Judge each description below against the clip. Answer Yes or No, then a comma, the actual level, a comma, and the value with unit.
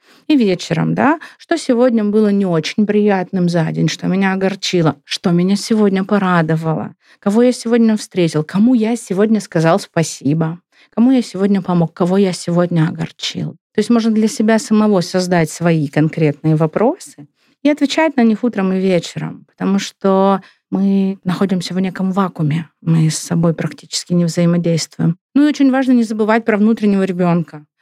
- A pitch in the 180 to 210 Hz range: Yes, high, 190 Hz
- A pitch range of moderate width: Yes, average, 4.5 semitones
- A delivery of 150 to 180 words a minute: Yes, fast, 160 wpm